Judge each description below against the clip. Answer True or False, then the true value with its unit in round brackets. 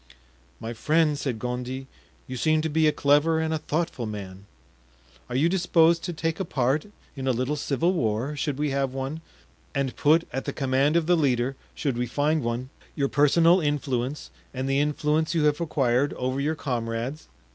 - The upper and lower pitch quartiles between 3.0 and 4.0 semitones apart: True (3.6 semitones)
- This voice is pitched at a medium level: True (145 Hz)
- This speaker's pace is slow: False (185 wpm)